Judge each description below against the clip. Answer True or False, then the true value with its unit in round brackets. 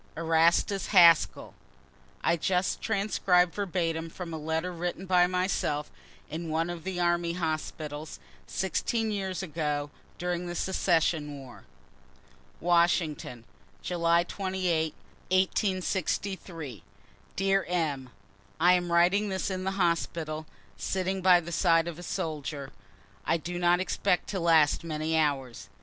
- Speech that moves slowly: True (125 wpm)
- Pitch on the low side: False (170 Hz)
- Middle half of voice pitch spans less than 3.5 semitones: True (2.4 semitones)